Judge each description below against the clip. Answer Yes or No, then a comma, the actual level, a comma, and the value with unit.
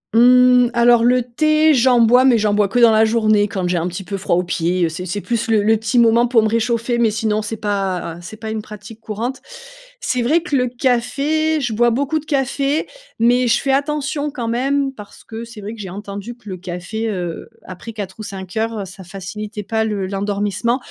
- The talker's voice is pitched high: Yes, high, 225 Hz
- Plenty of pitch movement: No, average, 3.5 semitones